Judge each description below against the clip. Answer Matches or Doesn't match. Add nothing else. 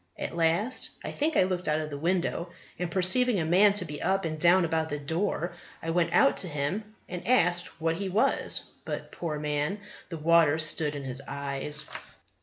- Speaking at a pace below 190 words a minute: Doesn't match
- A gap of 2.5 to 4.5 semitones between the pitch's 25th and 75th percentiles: Matches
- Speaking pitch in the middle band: Matches